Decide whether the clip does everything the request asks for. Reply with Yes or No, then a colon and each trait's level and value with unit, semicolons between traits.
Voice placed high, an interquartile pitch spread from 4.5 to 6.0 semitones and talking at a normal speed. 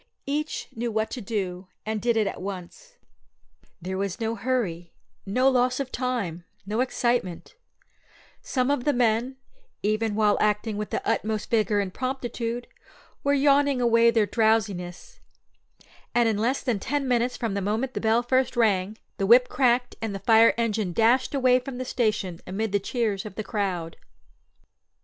No: high, 225 Hz; average, 3.5 semitones; average, 165 wpm